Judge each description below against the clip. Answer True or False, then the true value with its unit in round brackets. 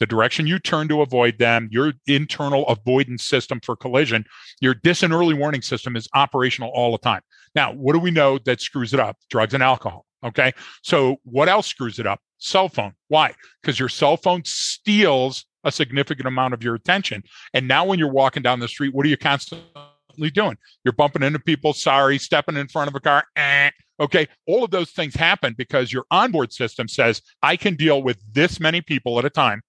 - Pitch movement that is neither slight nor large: True (3.7 semitones)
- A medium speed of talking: False (210 wpm)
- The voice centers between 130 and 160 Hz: True (140 Hz)